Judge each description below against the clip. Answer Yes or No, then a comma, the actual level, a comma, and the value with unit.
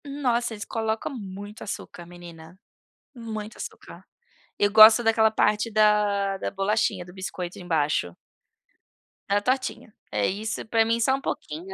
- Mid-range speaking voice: No, high, 210 Hz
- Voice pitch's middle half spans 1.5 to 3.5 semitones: Yes, average, 3.2 semitones